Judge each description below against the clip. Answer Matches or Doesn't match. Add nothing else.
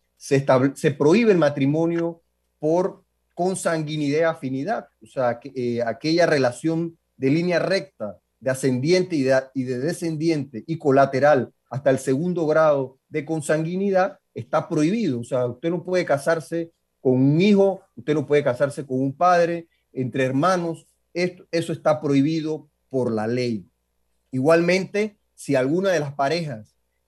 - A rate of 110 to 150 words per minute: Matches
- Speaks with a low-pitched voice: Doesn't match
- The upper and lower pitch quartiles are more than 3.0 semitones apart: Matches